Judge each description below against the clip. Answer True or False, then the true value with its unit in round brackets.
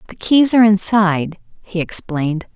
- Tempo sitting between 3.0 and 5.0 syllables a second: False (5.2 syllables/s)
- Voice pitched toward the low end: False (195 Hz)